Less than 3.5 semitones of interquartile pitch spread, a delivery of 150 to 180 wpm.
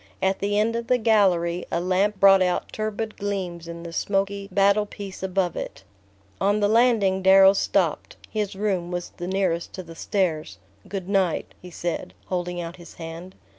Yes: narrow, 2.5 semitones; average, 175 wpm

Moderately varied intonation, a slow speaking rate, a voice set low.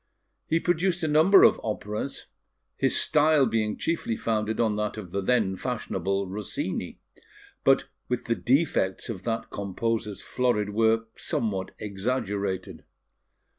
Yes: average, 3.9 semitones; slow, 130 wpm; low, 110 Hz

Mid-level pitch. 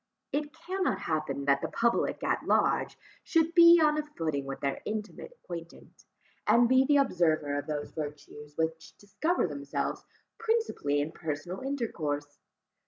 Yes: medium, 170 Hz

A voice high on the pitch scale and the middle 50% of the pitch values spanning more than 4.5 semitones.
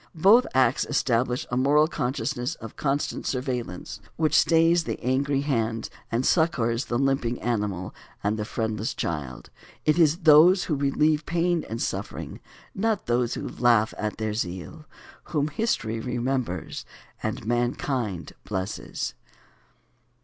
No: low, 125 Hz; average, 5.1 semitones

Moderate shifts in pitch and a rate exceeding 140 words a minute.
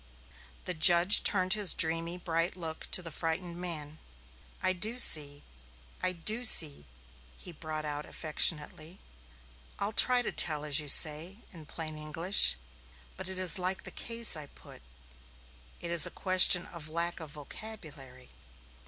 Yes: average, 3.3 semitones; average, 150 wpm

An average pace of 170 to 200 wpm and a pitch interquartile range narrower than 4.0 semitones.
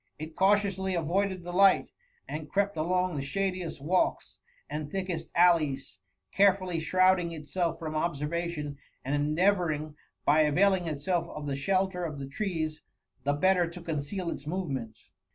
No: average, 140 wpm; average, 3.6 semitones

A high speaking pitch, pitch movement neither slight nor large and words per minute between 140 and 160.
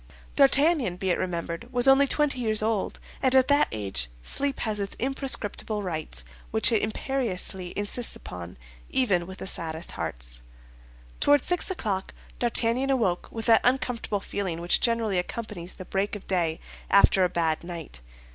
No: high, 205 Hz; wide, 6.2 semitones; average, 155 wpm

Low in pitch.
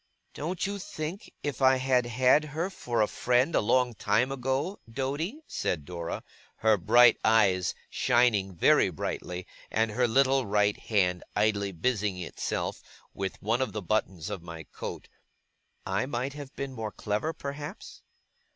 Yes: low, 120 Hz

